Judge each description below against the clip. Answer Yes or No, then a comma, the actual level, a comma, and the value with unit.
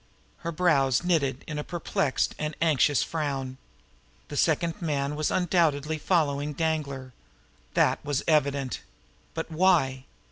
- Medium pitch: Yes, medium, 150 Hz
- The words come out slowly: Yes, slow, 120 wpm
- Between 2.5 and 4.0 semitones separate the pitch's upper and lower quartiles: Yes, average, 2.9 semitones